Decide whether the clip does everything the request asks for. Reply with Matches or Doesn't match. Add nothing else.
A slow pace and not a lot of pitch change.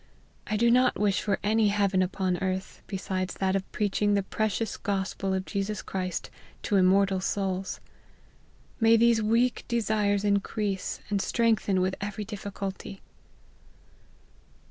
Matches